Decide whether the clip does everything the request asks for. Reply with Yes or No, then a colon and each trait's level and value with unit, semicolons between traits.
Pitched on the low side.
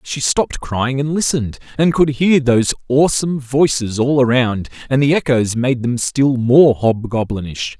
Yes: low, 130 Hz